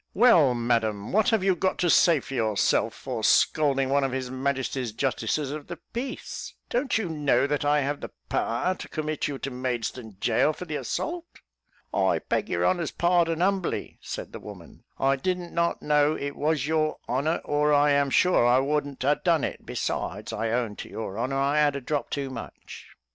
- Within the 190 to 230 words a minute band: Yes, average, 195 wpm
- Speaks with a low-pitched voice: No, medium, 145 Hz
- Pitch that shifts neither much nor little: Yes, average, 4.1 semitones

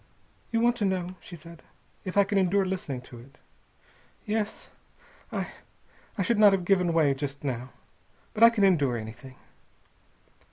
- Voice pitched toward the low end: No, medium, 180 Hz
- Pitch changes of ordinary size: No, wide, 6.5 semitones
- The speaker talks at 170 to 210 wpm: No, average, 160 wpm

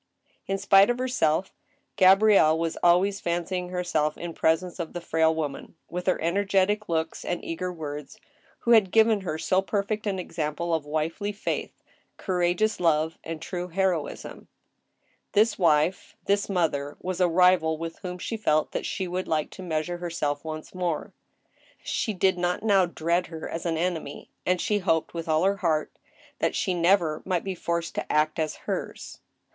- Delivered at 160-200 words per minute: Yes, average, 175 wpm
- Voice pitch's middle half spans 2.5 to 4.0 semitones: Yes, average, 3.1 semitones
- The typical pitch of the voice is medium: Yes, medium, 175 Hz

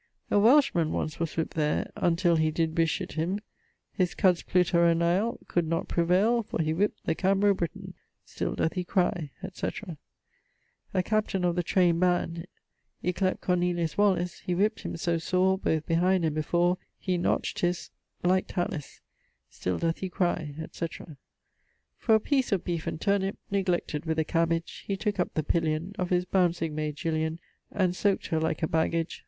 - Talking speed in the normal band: Yes, average, 175 wpm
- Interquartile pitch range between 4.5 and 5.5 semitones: No, narrow, 2.4 semitones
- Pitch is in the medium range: Yes, medium, 175 Hz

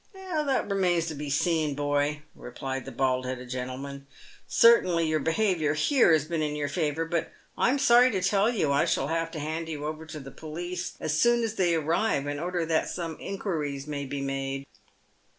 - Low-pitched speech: No, medium, 155 Hz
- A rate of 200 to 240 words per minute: Yes, fast, 205 wpm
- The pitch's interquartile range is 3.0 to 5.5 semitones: Yes, average, 3.9 semitones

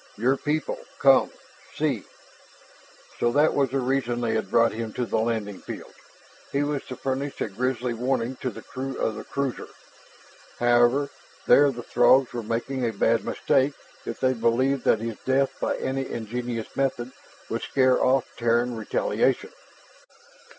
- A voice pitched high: No, low, 125 Hz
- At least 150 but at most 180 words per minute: Yes, average, 160 wpm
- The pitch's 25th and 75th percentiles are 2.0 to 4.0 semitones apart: Yes, narrow, 2.6 semitones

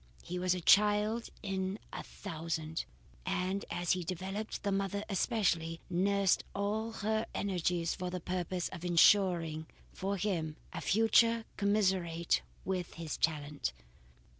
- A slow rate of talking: Yes, slow, 130 wpm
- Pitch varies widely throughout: No, average, 3.0 semitones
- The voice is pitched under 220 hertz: Yes, medium, 185 Hz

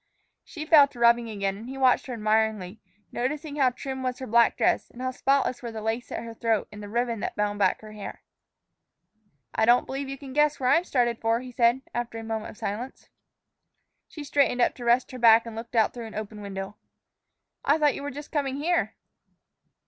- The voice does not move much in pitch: No, average, 3.3 semitones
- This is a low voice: No, high, 240 Hz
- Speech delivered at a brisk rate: Yes, fast, 215 wpm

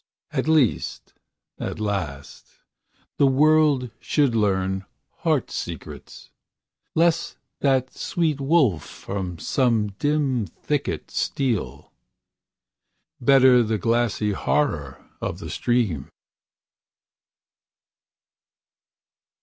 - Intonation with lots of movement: Yes, wide, 6.0 semitones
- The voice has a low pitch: Yes, low, 125 Hz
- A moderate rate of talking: No, slow, 80 wpm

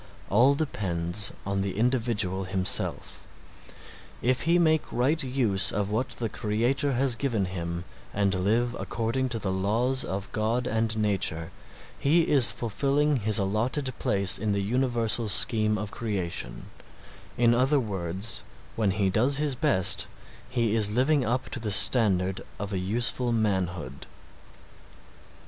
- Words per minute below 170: Yes, average, 140 wpm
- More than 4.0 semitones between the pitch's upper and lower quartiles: Yes, average, 4.4 semitones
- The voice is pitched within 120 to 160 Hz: No, low, 110 Hz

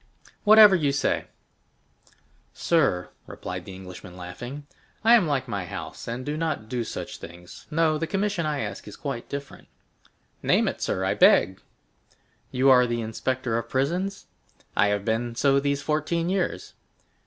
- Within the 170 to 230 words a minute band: No, average, 155 wpm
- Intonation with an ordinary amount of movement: No, wide, 5.9 semitones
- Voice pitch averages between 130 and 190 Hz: Yes, low, 135 Hz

